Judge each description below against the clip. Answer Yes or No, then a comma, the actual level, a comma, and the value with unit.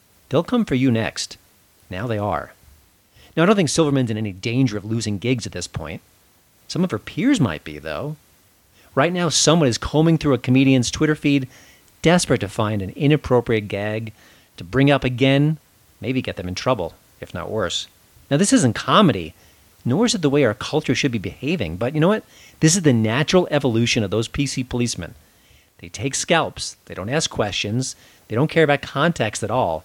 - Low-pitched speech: Yes, low, 125 Hz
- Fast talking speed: No, average, 195 wpm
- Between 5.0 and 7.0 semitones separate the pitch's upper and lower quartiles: Yes, wide, 5.6 semitones